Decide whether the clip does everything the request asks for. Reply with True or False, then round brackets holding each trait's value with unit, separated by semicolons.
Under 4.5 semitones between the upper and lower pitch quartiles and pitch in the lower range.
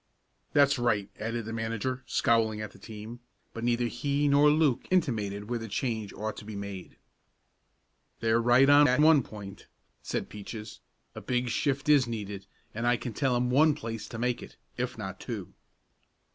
True (3.6 semitones; 115 Hz)